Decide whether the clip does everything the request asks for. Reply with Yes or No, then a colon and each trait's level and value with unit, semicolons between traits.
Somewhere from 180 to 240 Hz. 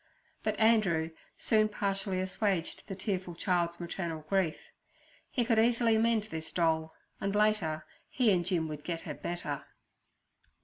Yes: medium, 185 Hz